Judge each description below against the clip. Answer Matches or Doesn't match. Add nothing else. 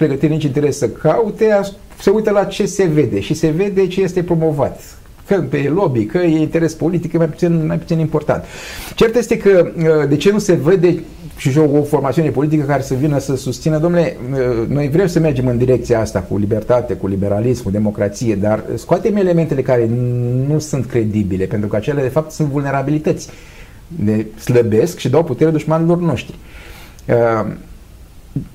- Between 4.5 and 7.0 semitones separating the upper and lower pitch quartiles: Matches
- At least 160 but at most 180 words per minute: Matches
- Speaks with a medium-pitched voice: Matches